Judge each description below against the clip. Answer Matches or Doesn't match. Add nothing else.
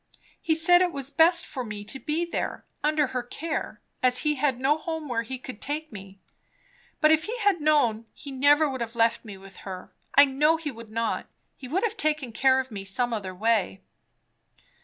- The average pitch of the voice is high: Matches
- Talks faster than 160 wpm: Matches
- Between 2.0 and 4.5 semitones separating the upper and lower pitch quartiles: Doesn't match